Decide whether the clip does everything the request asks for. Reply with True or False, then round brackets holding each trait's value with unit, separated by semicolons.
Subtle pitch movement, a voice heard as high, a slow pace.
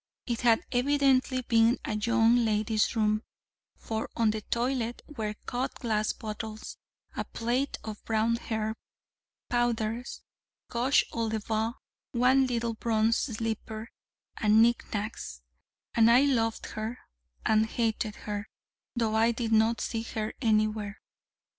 True (1.7 semitones; 225 Hz; 130 wpm)